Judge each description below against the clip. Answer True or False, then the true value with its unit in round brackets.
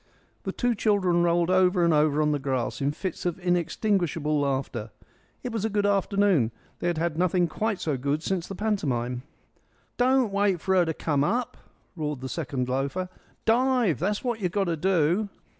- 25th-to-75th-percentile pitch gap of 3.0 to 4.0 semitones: False (5.2 semitones)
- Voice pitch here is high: False (175 Hz)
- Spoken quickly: False (185 wpm)